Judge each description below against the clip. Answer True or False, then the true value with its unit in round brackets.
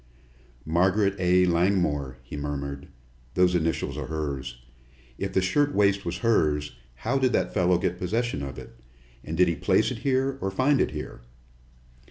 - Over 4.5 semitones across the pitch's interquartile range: True (5.2 semitones)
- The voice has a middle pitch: False (90 Hz)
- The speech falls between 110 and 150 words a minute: False (160 wpm)